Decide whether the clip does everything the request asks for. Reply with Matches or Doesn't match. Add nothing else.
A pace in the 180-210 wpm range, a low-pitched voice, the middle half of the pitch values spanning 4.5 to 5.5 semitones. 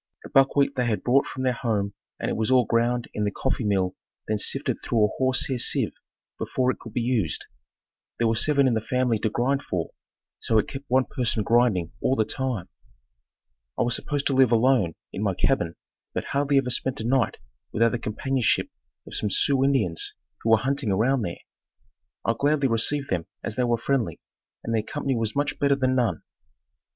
Doesn't match